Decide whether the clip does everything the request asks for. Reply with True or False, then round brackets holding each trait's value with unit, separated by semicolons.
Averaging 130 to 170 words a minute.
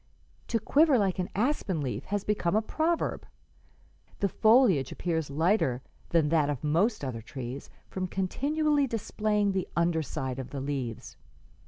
True (150 wpm)